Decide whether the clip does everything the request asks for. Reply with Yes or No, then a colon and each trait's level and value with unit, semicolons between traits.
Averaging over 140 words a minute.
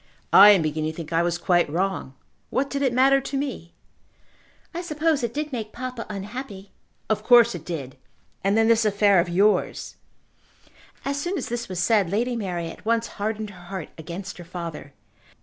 Yes: average, 185 wpm